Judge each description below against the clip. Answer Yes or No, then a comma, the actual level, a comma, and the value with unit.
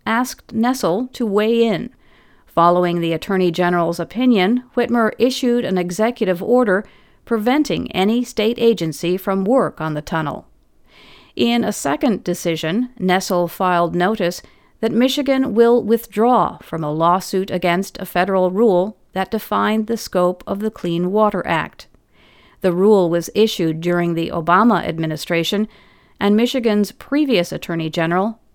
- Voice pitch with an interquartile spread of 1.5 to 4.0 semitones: No, average, 4.7 semitones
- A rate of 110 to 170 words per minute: Yes, slow, 135 wpm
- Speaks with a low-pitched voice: No, high, 195 Hz